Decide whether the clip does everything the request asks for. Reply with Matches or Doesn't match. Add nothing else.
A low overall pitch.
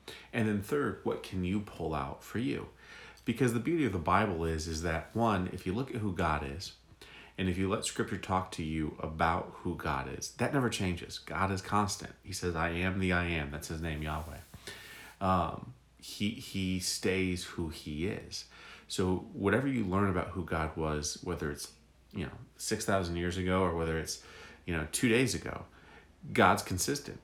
Matches